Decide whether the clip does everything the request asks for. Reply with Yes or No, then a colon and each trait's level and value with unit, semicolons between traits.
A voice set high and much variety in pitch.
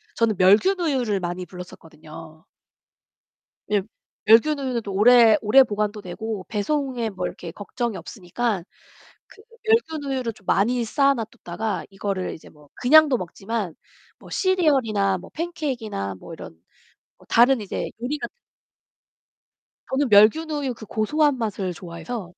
Yes: high, 220 Hz; wide, 5.7 semitones